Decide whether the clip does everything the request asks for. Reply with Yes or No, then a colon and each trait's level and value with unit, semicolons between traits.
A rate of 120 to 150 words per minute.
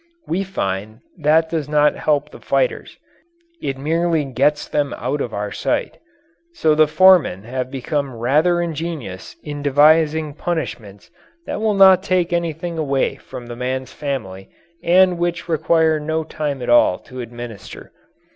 Yes: average, 145 wpm